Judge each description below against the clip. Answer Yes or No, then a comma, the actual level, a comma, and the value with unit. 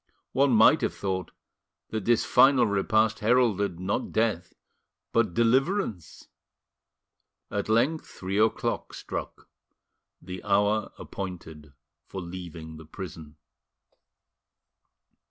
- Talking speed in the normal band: No, slow, 100 wpm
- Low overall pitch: Yes, low, 100 Hz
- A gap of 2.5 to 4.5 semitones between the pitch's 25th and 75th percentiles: Yes, average, 4.1 semitones